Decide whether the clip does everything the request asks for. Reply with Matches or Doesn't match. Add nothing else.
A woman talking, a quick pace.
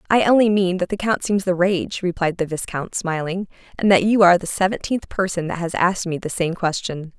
Matches